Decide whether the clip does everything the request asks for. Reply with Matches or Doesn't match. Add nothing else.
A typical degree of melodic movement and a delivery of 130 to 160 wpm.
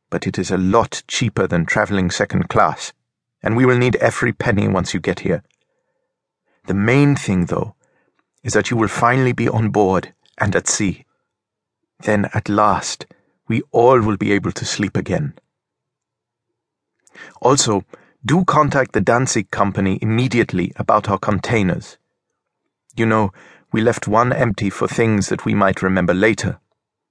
Matches